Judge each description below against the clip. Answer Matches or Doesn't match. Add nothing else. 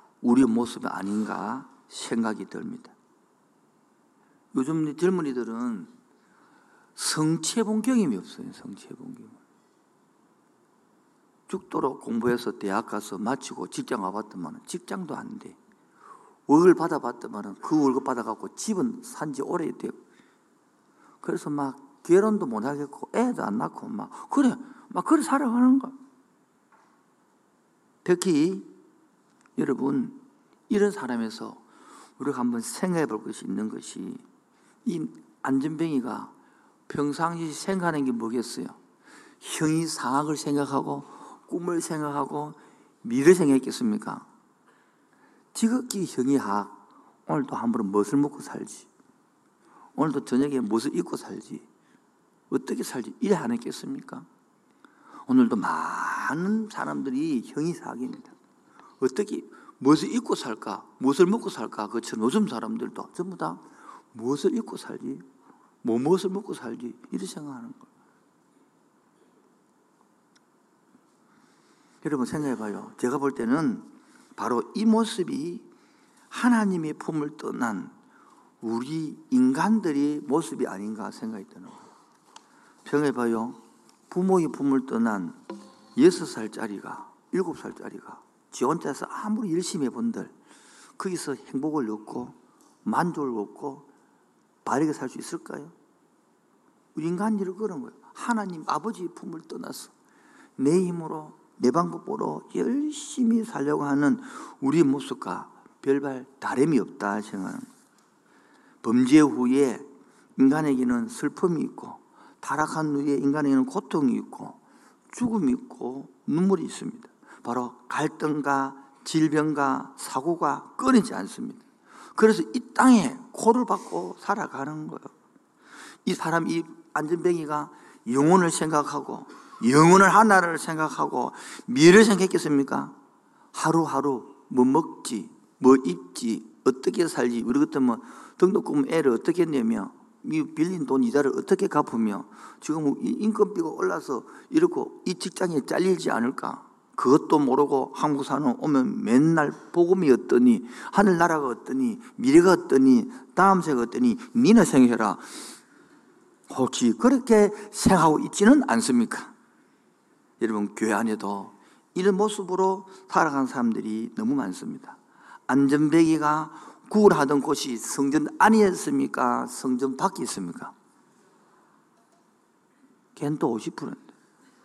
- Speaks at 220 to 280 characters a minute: Matches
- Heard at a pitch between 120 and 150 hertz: Doesn't match